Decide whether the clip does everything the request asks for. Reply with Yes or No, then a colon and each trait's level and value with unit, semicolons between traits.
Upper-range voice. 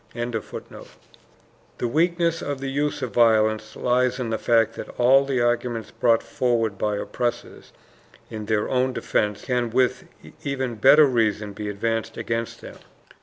No: low, 120 Hz